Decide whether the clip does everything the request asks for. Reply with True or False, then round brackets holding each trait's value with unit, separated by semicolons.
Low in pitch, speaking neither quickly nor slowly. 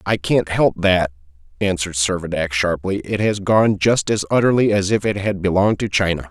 True (95 Hz; 190 wpm)